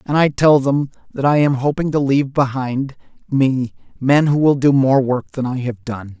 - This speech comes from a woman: No, male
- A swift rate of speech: Yes, fast, 215 wpm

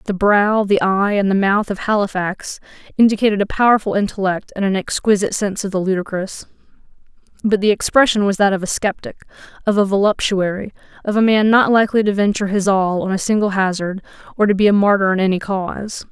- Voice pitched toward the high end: Yes, high, 200 Hz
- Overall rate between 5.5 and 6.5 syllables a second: Yes, 6.1 syllables/s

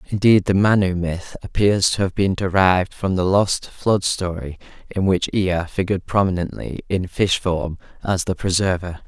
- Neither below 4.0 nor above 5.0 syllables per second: Yes, 4.8 syllables/s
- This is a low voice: Yes, very low, 95 Hz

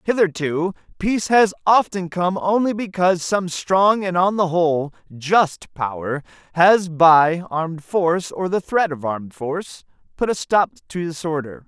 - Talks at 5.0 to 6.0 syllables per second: No, 4.5 syllables/s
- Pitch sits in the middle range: Yes, medium, 175 Hz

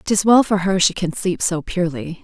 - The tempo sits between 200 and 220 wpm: No, fast, 240 wpm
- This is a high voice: No, medium, 180 Hz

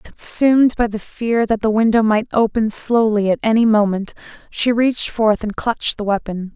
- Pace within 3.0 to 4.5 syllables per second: No, 5.0 syllables/s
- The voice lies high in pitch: Yes, high, 220 Hz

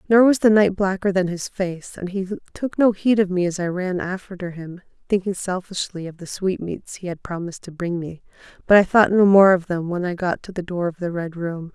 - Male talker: No, female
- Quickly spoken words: Yes, fast, 240 wpm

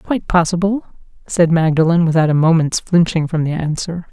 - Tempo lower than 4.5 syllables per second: No, 5.5 syllables/s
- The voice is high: No, medium, 165 Hz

